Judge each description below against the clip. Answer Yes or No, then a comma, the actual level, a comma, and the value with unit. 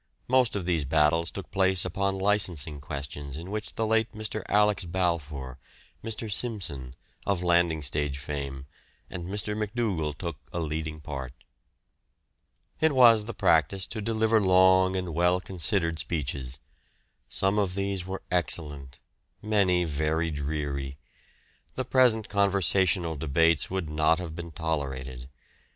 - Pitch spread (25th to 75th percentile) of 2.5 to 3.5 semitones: No, average, 4.9 semitones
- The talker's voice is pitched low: Yes, very low, 85 Hz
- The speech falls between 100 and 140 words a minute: Yes, slow, 135 wpm